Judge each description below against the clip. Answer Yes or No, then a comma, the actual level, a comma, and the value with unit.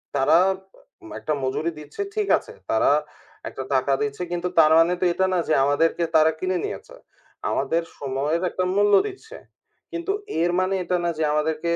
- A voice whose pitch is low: No, medium, 165 Hz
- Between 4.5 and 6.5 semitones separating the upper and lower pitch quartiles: No, average, 3.6 semitones